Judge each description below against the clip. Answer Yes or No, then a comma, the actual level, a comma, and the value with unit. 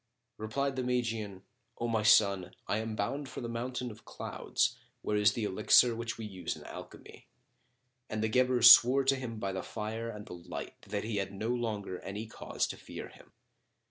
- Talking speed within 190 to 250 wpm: Yes, average, 195 wpm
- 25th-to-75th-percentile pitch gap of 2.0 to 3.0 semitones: Yes, average, 2.7 semitones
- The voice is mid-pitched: No, low, 110 Hz